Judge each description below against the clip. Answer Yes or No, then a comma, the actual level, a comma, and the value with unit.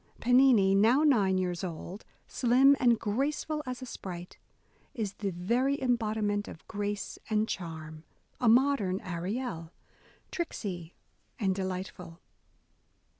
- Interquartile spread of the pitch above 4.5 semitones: Yes, average, 5.2 semitones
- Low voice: No, high, 205 Hz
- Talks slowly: Yes, slow, 120 wpm